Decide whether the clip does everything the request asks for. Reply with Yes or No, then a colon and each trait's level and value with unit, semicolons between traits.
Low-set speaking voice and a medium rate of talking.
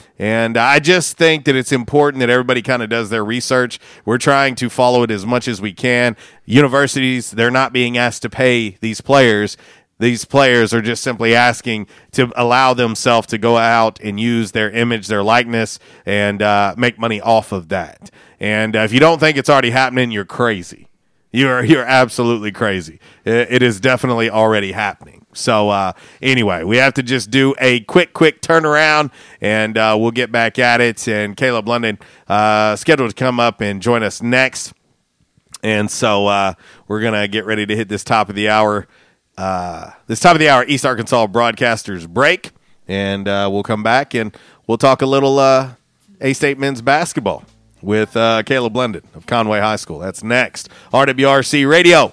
Yes: low, 120 Hz; average, 185 wpm